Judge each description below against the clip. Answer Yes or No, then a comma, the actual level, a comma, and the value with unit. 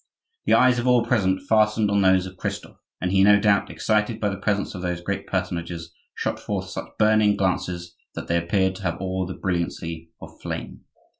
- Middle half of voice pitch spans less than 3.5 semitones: Yes, average, 2.8 semitones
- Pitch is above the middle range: No, very low, 95 Hz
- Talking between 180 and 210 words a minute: Yes, average, 200 wpm